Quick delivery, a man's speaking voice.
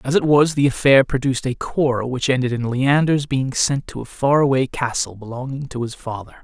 Yes: fast, 215 wpm; male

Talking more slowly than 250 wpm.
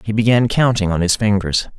Yes: average, 200 wpm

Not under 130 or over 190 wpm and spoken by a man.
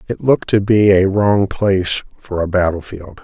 No: fast, 205 wpm; male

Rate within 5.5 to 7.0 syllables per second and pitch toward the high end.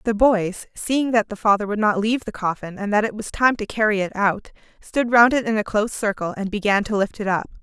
Yes: 5.7 syllables/s; high, 210 Hz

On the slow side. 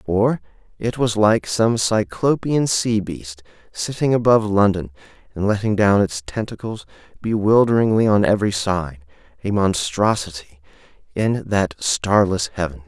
Yes: slow, 120 wpm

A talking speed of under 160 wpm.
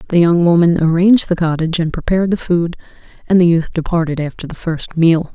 No: average, 200 wpm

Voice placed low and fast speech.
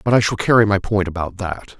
Yes: low, 100 Hz; fast, 265 wpm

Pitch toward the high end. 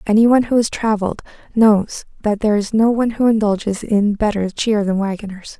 Yes: high, 215 Hz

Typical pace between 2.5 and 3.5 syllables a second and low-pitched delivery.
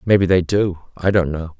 No: 5.1 syllables/s; very low, 90 Hz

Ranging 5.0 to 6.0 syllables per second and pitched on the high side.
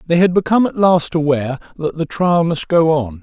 No: 5.5 syllables/s; medium, 160 Hz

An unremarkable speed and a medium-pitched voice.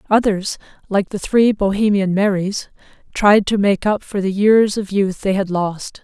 No: average, 180 wpm; high, 200 Hz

